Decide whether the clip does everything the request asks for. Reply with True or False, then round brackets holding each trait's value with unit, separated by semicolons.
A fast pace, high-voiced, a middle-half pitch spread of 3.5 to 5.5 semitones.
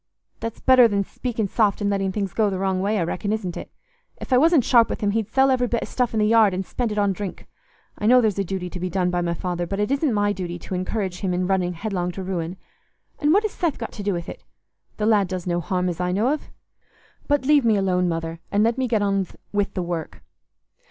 True (260 wpm; 200 Hz; 3.8 semitones)